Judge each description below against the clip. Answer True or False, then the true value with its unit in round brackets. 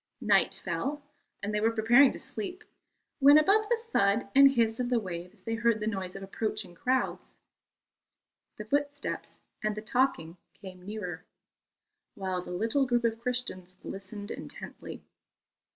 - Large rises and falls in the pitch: False (5.0 semitones)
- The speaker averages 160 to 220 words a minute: False (150 wpm)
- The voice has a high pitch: True (220 Hz)